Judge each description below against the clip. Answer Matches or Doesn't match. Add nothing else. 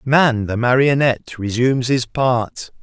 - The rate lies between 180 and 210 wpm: Doesn't match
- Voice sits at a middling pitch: Doesn't match